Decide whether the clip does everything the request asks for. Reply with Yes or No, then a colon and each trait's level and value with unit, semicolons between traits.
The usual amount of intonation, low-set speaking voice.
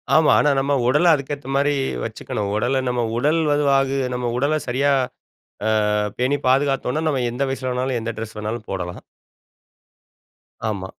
Yes: average, 3.0 semitones; low, 130 Hz